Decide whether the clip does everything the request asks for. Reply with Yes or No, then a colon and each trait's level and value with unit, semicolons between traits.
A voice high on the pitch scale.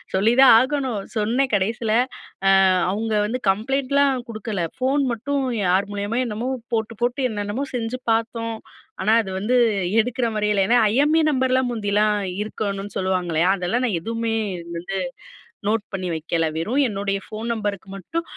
Yes: high, 220 Hz